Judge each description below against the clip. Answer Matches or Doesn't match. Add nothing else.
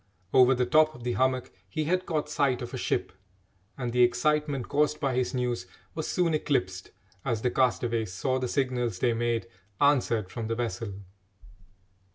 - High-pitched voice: Doesn't match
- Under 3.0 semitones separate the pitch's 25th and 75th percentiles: Doesn't match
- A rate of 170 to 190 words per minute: Matches